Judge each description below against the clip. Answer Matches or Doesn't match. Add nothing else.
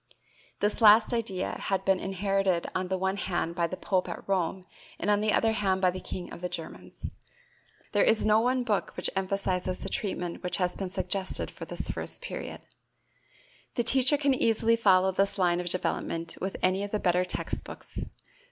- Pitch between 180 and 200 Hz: Matches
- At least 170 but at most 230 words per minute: Matches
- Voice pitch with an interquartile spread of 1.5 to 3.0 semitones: Matches